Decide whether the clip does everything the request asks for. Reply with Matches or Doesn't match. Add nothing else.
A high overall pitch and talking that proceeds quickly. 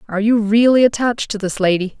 Matches